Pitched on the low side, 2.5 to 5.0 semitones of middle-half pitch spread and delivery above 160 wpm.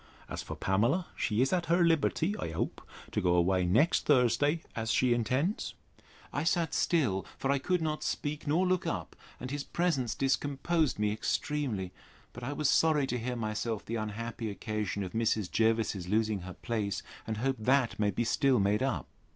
No: low, 120 Hz; wide, 5.5 semitones; average, 185 wpm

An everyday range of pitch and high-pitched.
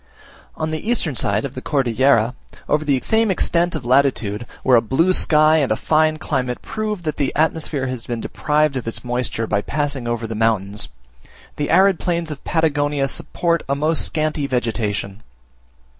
No: average, 4.8 semitones; medium, 140 Hz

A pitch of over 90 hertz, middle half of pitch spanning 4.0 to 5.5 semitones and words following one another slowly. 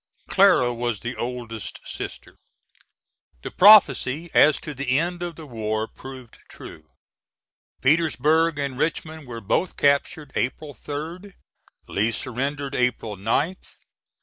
Yes: medium, 140 Hz; average, 4.8 semitones; slow, 120 wpm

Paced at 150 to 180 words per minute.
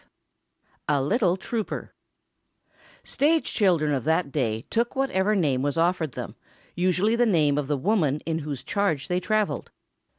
Yes: average, 155 wpm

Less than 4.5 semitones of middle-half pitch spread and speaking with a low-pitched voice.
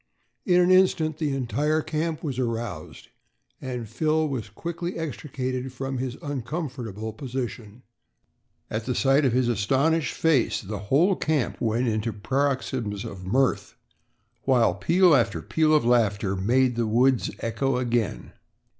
No: average, 4.8 semitones; low, 130 Hz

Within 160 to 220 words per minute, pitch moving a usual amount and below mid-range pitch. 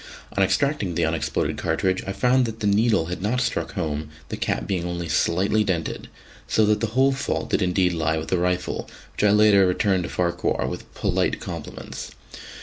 Yes: average, 190 wpm; average, 3.7 semitones; very low, 95 Hz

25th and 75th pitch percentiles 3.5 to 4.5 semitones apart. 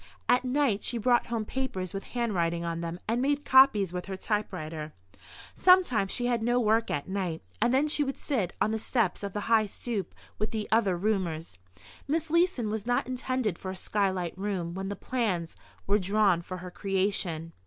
No: average, 4.9 semitones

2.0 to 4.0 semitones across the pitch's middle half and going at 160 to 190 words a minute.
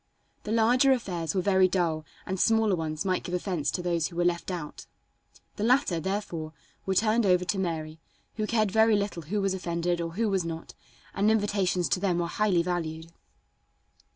Yes: average, 3.6 semitones; average, 185 wpm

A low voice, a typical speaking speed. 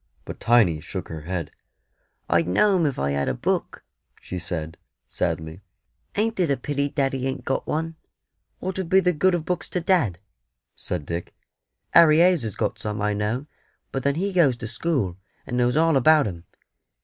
Yes: low, 130 Hz; average, 185 wpm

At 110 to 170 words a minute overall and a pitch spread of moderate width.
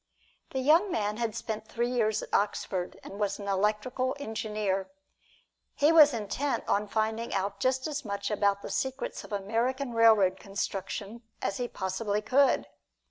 Yes: average, 155 wpm; average, 4.0 semitones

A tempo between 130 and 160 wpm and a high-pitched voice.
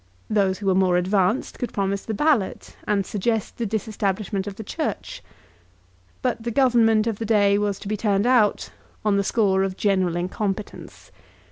No: average, 170 wpm; high, 205 Hz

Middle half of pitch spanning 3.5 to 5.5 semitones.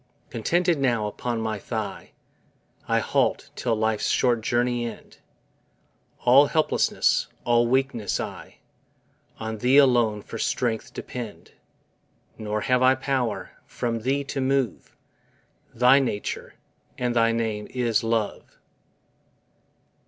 No: average, 2.8 semitones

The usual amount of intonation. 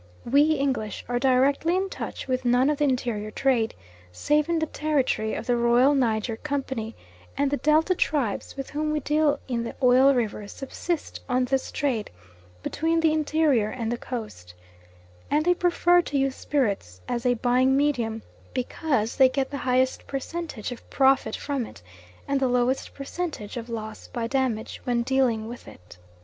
Yes: average, 3.6 semitones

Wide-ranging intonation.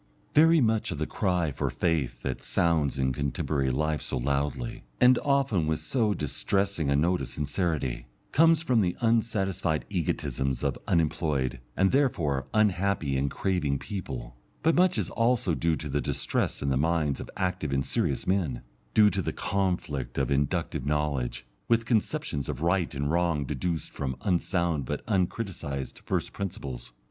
Yes: wide, 6.0 semitones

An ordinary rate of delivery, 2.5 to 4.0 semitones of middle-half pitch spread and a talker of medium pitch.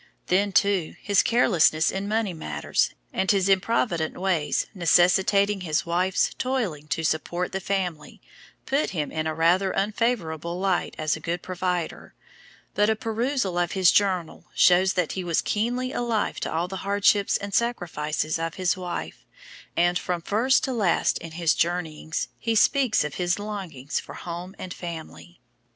Yes: average, 160 wpm; average, 3.5 semitones; medium, 180 Hz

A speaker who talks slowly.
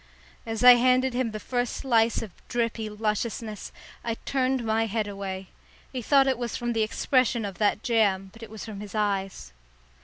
No: average, 185 wpm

